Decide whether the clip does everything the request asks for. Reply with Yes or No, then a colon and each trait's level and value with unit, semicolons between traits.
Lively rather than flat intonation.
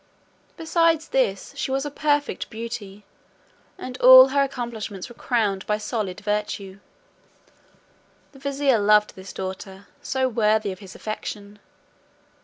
No: average, 4.9 semitones